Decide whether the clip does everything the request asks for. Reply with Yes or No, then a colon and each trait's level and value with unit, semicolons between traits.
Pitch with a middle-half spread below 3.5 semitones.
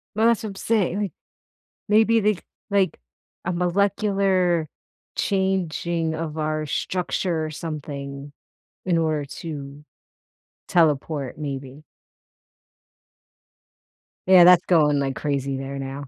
No: average, 4.7 semitones